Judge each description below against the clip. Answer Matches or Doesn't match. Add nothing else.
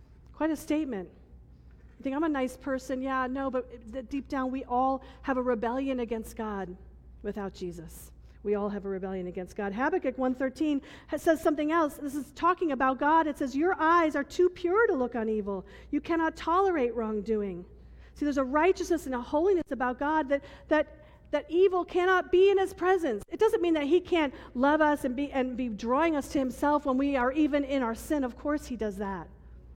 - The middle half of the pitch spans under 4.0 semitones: Doesn't match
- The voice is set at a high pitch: Matches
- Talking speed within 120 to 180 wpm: Doesn't match